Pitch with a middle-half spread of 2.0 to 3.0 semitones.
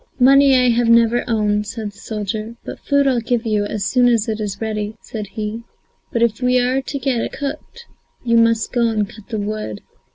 Yes: narrow, 2.6 semitones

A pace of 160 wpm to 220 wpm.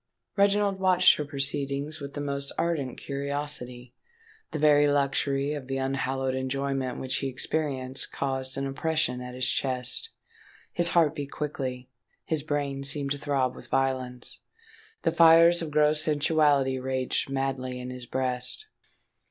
No: average, 145 wpm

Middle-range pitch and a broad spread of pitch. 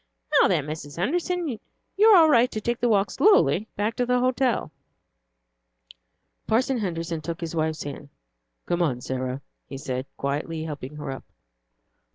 Yes: medium, 175 Hz; wide, 8.9 semitones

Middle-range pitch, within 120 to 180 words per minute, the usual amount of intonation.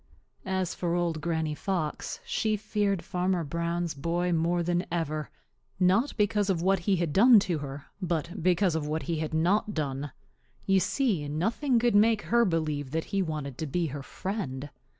Yes: medium, 175 Hz; average, 175 wpm; average, 3.9 semitones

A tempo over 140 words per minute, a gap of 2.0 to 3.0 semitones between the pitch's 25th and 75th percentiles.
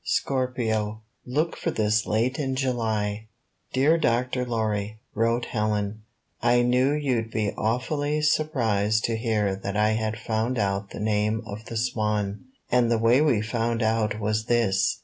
Yes: average, 150 wpm; average, 2.7 semitones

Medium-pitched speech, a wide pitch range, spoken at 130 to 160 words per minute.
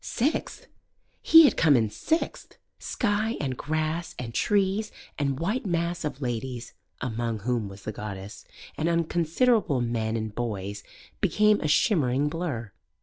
Yes: medium, 145 Hz; wide, 7.3 semitones; average, 140 wpm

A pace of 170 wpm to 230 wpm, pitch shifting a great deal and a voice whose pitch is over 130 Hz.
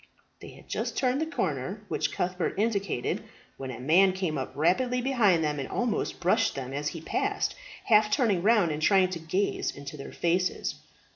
Yes: average, 185 wpm; wide, 5.8 semitones; medium, 185 Hz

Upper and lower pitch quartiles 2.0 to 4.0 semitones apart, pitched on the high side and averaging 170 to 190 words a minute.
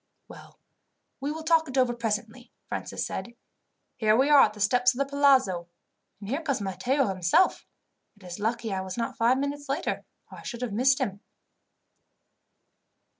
No: average, 4.8 semitones; high, 240 Hz; average, 175 wpm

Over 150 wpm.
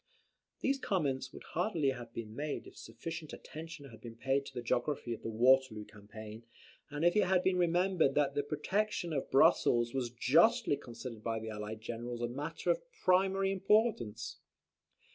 Yes: average, 170 wpm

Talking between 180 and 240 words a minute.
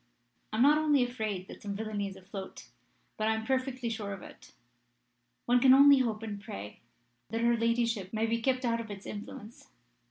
Yes: average, 195 wpm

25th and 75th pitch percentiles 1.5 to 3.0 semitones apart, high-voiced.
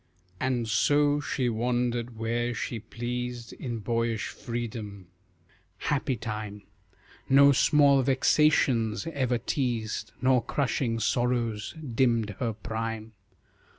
No: narrow, 2.6 semitones; low, 120 Hz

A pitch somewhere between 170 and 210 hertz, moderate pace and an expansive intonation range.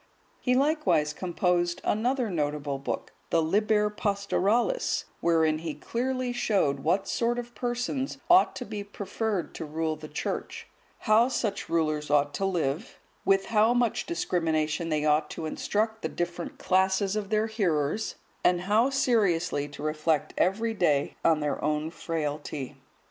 Yes: medium, 185 Hz; average, 145 wpm; wide, 6.2 semitones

